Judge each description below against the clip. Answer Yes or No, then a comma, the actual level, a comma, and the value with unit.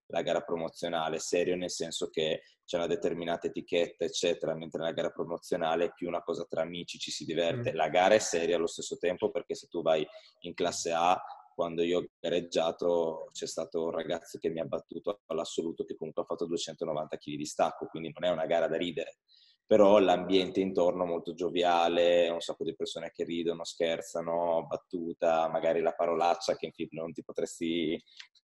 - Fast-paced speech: Yes, fast, 190 wpm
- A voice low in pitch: Yes, very low, 85 Hz